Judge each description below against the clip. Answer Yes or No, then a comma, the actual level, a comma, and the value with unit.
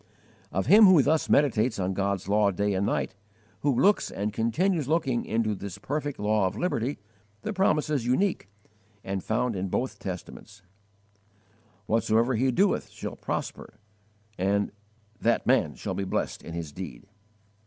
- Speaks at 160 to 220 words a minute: No, average, 150 wpm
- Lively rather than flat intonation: Yes, wide, 6.2 semitones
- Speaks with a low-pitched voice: Yes, low, 110 Hz